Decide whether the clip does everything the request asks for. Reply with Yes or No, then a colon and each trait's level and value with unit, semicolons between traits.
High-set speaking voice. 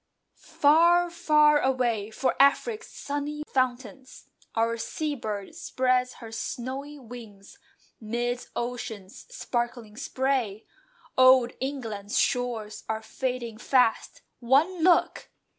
Yes: very high, 250 Hz